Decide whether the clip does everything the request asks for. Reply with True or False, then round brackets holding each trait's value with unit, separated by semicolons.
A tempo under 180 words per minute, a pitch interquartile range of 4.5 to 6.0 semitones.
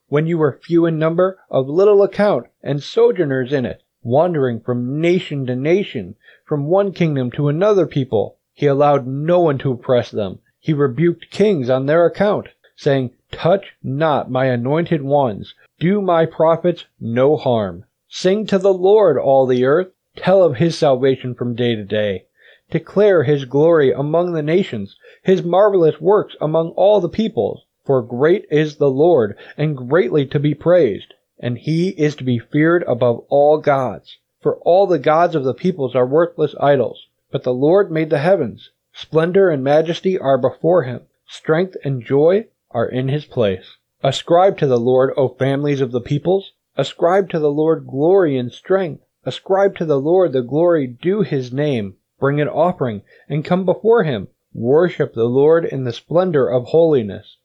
True (170 wpm; 4.9 semitones)